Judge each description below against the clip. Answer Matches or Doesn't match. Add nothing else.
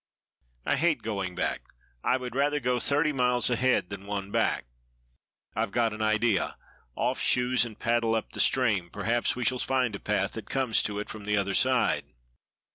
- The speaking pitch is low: Matches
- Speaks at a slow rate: Doesn't match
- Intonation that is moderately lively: Matches